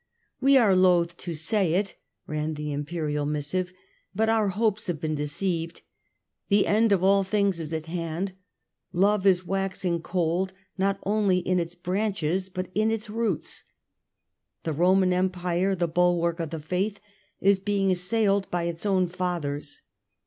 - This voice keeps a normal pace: Yes, average, 160 wpm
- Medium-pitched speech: Yes, medium, 180 Hz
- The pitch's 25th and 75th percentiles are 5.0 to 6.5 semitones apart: No, average, 2.8 semitones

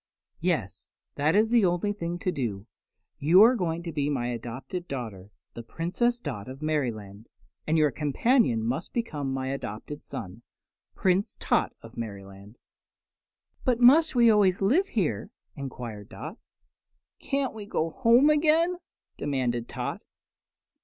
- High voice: No, medium, 155 Hz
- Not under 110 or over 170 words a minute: Yes, average, 140 wpm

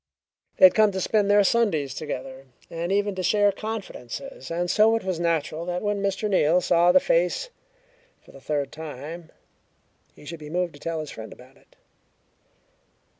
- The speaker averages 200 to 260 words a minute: No, average, 175 wpm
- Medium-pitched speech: Yes, medium, 175 Hz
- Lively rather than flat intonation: No, average, 4.7 semitones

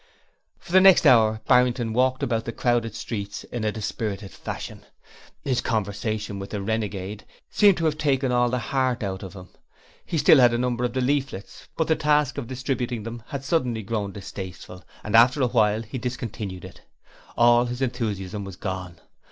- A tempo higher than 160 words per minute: Yes, average, 185 wpm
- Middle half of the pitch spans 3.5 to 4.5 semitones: Yes, average, 3.8 semitones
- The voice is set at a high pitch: No, low, 120 Hz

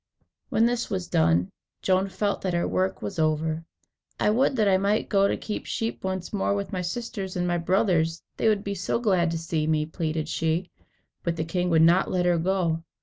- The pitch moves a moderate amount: Yes, average, 3.3 semitones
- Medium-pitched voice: Yes, medium, 180 Hz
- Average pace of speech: No, fast, 210 wpm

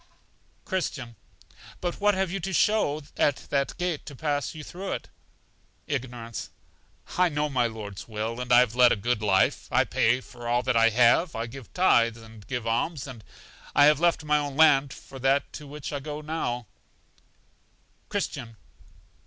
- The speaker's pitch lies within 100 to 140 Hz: Yes, low, 135 Hz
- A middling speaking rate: Yes, average, 170 wpm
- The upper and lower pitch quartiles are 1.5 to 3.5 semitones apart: No, average, 4.5 semitones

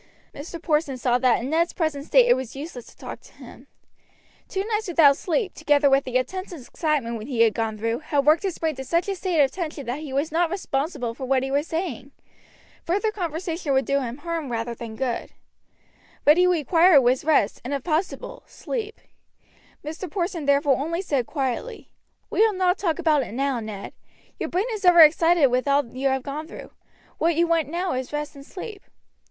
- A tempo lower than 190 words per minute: No, fast, 205 wpm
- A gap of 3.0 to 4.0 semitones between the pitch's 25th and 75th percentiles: No, average, 4.6 semitones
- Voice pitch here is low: No, very high, 300 Hz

